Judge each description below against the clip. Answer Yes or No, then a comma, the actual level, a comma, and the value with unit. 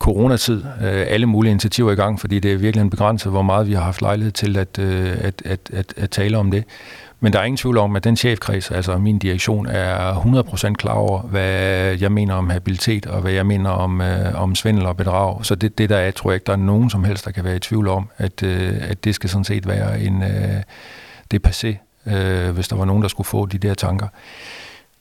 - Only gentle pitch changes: Yes, narrow, 1.9 semitones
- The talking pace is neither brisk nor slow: No, fast, 230 wpm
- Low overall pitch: Yes, low, 100 Hz